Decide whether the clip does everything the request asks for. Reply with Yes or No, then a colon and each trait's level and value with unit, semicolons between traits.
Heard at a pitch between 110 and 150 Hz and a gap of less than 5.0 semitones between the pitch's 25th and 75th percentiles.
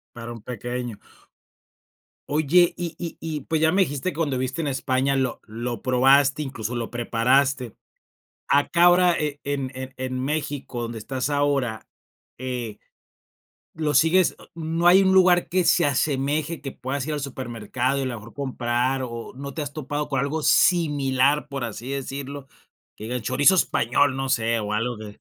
Yes: low, 135 Hz; average, 3.4 semitones